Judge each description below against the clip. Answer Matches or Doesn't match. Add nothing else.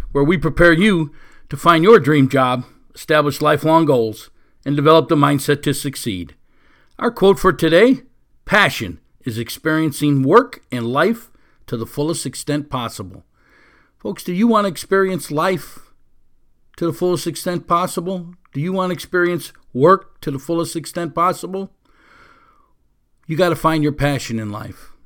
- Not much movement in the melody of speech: Doesn't match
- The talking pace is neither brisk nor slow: Matches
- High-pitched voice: Doesn't match